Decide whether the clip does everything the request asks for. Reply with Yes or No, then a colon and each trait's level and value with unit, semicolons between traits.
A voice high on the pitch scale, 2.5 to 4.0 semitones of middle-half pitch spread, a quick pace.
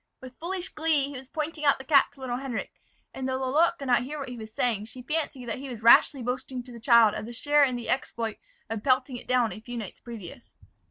Yes: very high, 255 Hz; average, 2.9 semitones; fast, 250 wpm